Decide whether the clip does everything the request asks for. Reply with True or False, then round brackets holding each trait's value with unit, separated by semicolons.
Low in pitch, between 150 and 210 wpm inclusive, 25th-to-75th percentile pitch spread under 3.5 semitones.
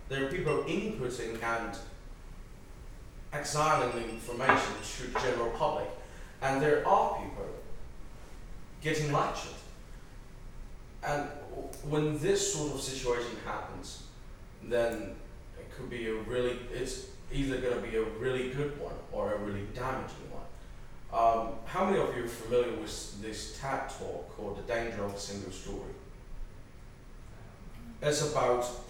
False (120 Hz; 135 wpm; 3.1 semitones)